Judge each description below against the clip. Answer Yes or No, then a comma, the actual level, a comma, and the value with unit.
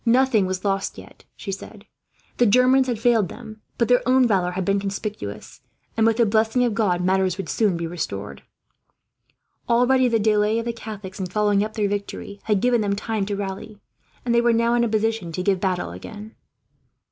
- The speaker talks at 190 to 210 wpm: Yes, average, 200 wpm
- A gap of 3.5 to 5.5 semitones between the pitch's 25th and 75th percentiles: No, average, 3.1 semitones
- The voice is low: No, high, 210 Hz